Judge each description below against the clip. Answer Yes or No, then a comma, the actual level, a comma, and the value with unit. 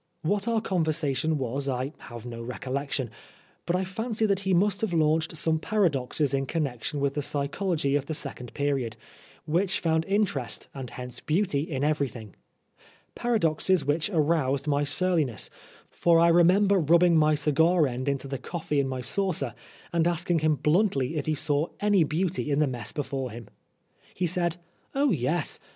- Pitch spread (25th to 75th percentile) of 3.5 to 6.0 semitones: Yes, average, 4.2 semitones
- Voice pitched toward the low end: No, medium, 155 Hz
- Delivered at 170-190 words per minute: Yes, average, 175 wpm